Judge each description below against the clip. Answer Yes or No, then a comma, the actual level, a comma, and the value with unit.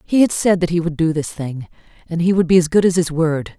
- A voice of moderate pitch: Yes, medium, 165 Hz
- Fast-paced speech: Yes, fast, 300 wpm